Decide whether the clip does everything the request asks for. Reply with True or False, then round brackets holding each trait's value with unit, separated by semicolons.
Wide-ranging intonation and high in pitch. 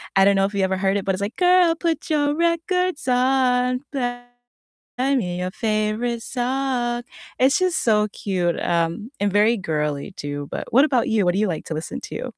True (5.7 semitones; 225 Hz)